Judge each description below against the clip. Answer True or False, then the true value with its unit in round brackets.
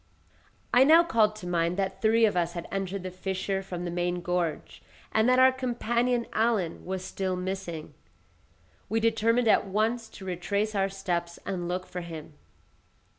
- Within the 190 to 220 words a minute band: False (170 wpm)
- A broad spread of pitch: False (4.0 semitones)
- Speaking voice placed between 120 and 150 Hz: False (195 Hz)